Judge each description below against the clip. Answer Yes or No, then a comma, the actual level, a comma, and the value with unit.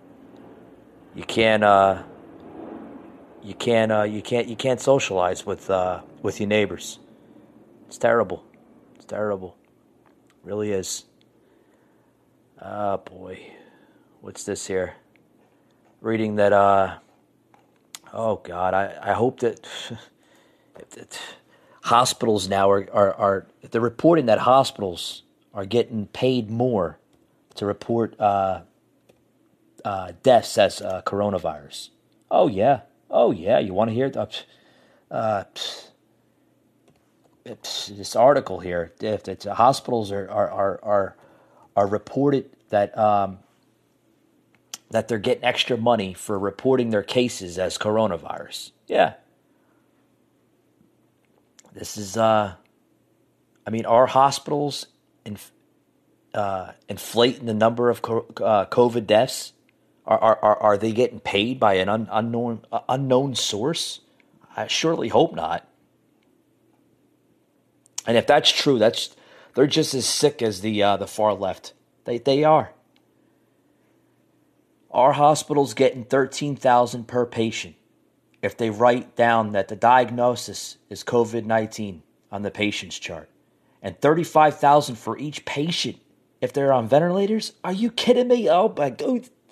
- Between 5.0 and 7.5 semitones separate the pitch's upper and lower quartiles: No, average, 4.0 semitones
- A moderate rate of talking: No, slow, 125 wpm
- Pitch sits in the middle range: No, low, 110 Hz